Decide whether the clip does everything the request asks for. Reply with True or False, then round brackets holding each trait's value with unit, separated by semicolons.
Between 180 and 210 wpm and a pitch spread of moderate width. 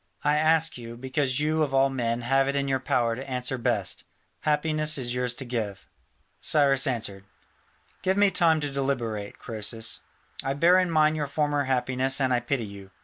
True (185 wpm; 3.6 semitones)